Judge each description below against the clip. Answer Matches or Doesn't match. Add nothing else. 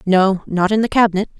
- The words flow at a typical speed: Matches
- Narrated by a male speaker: Doesn't match